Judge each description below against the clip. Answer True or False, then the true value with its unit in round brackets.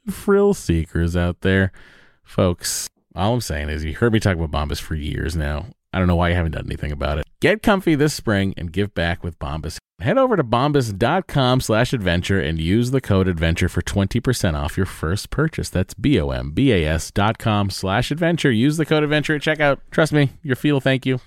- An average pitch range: False (8.4 semitones)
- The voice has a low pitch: True (100 Hz)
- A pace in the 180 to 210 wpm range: True (190 wpm)